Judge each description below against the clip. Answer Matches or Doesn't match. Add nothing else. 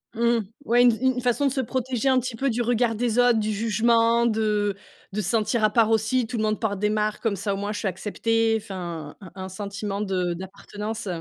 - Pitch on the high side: Matches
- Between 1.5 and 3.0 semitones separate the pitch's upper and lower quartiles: Matches